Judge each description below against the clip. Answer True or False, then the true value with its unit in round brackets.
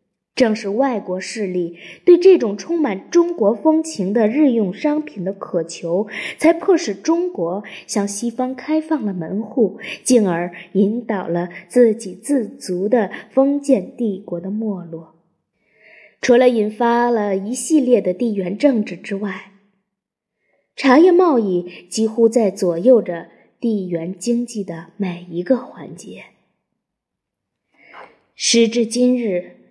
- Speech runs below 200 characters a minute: True (185 characters per minute)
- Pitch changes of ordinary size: True (4.9 semitones)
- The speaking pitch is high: True (215 Hz)